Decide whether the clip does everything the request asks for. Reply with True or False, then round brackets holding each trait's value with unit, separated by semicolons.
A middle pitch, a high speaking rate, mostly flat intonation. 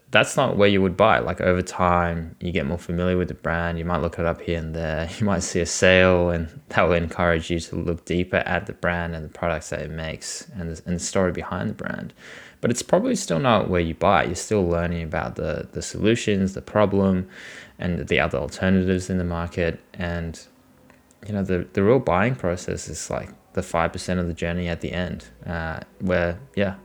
False (85 Hz; 215 wpm; 1.9 semitones)